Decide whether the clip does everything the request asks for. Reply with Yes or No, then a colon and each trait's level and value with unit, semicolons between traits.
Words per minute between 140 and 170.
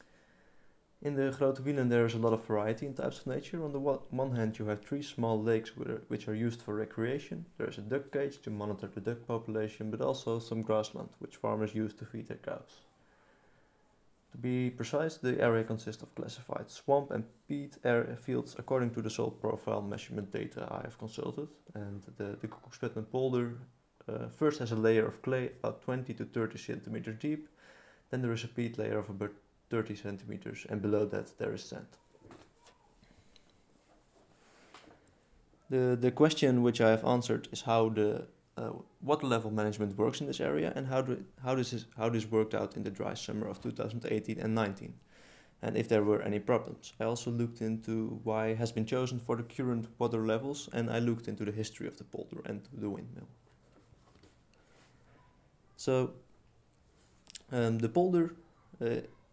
No: average, 185 wpm